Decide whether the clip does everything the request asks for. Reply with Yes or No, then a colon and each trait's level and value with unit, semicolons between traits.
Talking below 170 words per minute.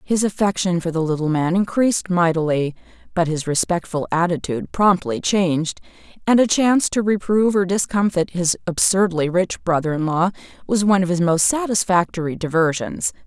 Yes: average, 155 wpm